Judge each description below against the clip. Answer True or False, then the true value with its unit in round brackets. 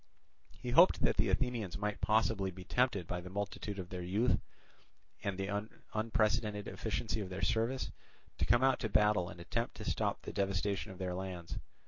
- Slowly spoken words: False (180 wpm)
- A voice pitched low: True (105 Hz)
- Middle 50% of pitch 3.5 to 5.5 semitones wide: False (3.0 semitones)